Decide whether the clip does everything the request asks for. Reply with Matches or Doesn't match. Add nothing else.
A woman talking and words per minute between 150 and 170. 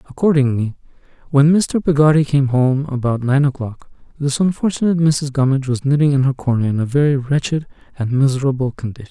Doesn't match